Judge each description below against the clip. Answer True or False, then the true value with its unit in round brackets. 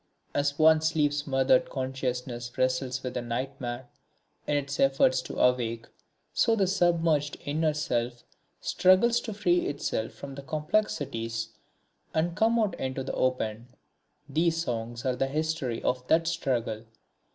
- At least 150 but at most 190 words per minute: False (140 wpm)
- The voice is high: False (135 Hz)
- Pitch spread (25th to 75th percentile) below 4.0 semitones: False (4.3 semitones)